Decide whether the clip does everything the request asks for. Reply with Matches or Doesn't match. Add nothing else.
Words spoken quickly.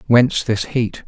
Doesn't match